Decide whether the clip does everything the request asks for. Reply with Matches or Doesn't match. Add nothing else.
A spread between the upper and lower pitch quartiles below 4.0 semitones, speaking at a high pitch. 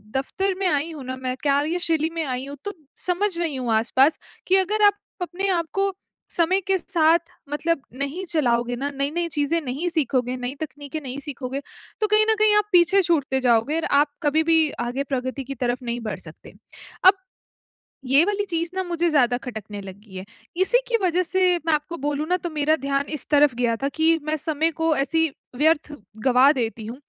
Doesn't match